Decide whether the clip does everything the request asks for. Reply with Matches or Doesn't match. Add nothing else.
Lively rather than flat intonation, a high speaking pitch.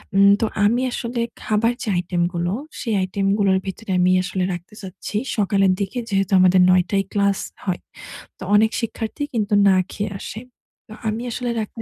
Doesn't match